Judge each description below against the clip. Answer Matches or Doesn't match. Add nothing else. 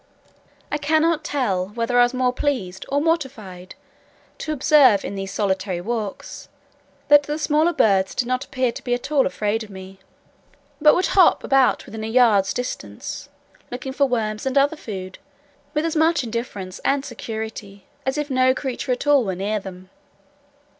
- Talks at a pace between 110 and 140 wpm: Doesn't match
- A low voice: Doesn't match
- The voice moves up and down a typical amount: Doesn't match